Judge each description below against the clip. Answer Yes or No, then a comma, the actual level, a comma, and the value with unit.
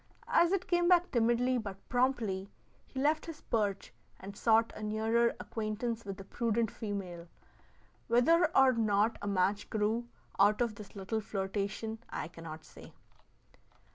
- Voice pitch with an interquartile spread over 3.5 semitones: No, average, 3.2 semitones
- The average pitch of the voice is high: Yes, high, 220 Hz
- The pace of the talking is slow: No, average, 145 wpm